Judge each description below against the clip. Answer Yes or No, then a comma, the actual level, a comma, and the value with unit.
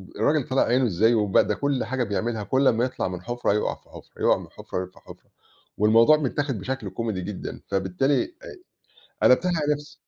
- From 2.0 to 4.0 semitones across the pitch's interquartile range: No, average, 4.8 semitones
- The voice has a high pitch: No, low, 120 Hz